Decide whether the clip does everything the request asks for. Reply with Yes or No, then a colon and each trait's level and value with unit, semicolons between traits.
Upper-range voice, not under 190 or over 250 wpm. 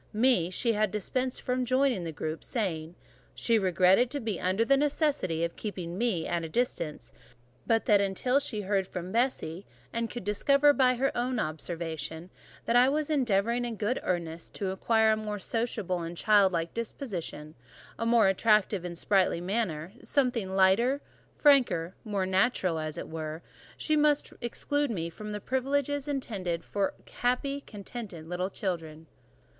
No: high, 210 Hz; average, 155 wpm